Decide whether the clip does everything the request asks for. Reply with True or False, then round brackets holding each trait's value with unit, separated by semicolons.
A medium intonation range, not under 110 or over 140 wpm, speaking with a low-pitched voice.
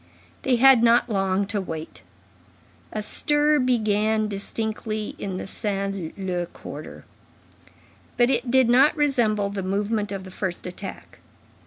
False (3.7 semitones; 135 wpm; 210 Hz)